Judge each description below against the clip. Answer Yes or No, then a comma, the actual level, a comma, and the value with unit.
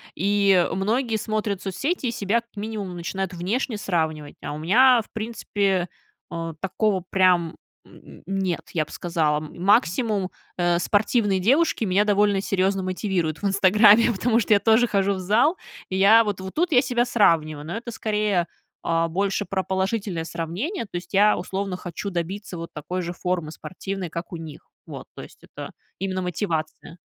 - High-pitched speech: Yes, high, 195 Hz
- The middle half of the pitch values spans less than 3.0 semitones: No, average, 3.5 semitones